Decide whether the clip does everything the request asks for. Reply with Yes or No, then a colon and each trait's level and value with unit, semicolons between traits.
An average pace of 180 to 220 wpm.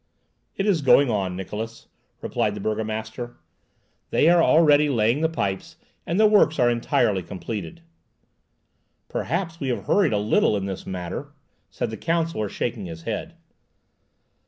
No: average, 145 wpm